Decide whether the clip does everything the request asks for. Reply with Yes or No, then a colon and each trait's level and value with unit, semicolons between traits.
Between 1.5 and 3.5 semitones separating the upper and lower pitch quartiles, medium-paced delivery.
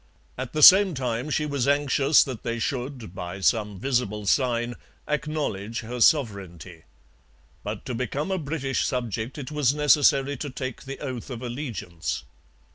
No: average, 4.0 semitones; average, 150 wpm